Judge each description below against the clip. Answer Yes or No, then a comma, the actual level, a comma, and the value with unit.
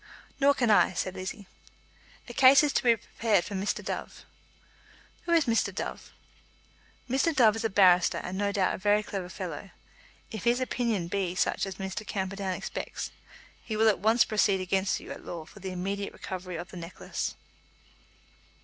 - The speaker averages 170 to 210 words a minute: Yes, average, 175 wpm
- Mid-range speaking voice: No, high, 200 Hz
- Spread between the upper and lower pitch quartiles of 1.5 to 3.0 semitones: No, average, 3.5 semitones